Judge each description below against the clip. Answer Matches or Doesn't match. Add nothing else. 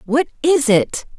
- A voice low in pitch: Doesn't match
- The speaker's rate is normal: Matches